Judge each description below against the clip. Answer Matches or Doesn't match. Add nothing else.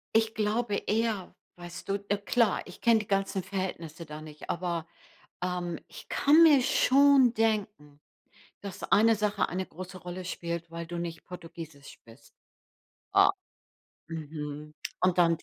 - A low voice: Doesn't match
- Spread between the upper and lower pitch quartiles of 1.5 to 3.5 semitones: Doesn't match